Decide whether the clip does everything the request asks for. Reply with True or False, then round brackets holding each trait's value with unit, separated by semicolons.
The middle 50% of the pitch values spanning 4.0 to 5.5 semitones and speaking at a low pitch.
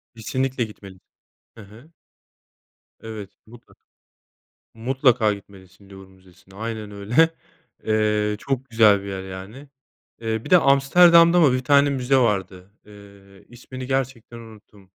True (4.7 semitones; 110 Hz)